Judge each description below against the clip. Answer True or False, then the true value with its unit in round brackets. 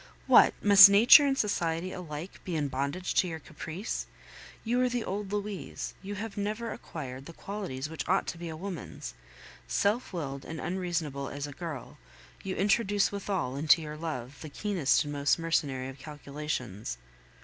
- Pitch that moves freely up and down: True (5.7 semitones)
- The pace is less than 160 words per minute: False (170 wpm)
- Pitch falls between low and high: True (165 Hz)